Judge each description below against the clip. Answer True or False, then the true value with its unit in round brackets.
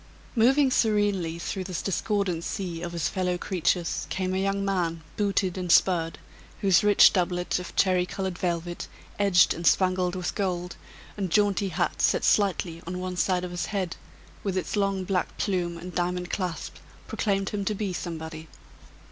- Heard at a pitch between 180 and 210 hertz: True (185 Hz)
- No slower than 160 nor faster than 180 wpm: True (165 wpm)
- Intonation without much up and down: True (2.1 semitones)